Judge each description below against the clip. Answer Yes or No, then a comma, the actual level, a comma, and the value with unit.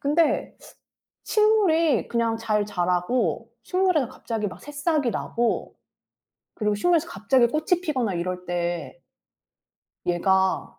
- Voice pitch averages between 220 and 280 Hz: Yes, high, 230 Hz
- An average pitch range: No, wide, 8.5 semitones